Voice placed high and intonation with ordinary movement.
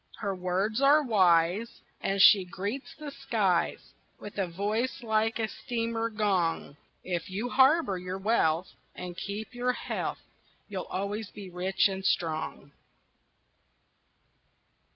Yes: high, 200 Hz; average, 3.9 semitones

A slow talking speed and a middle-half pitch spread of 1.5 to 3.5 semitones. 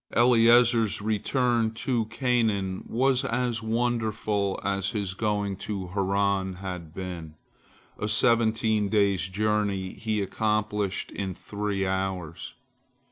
Yes: slow, 105 wpm; average, 2.8 semitones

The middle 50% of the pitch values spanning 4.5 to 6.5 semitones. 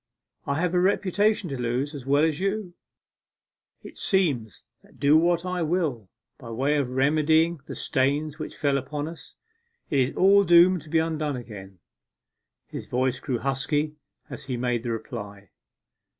Yes: average, 4.9 semitones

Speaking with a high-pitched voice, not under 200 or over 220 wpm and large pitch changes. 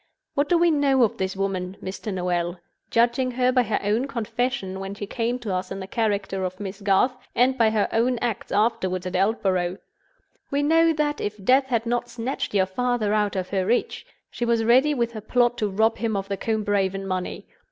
No: high, 220 Hz; fast, 205 wpm; average, 4.2 semitones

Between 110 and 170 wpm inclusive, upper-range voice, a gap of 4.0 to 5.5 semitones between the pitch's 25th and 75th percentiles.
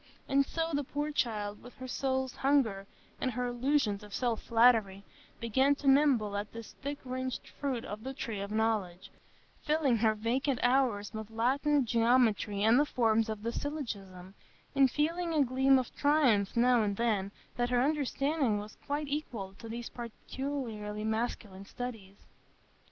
Yes: average, 160 wpm; high, 240 Hz; average, 4.3 semitones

